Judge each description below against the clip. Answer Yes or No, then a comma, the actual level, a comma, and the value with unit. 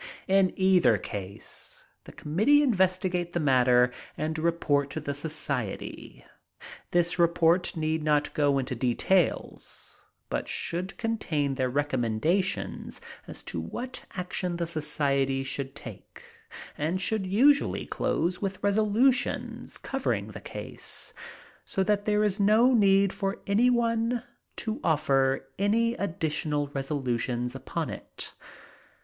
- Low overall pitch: No, medium, 170 Hz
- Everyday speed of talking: No, slow, 120 wpm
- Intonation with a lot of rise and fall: Yes, wide, 6.2 semitones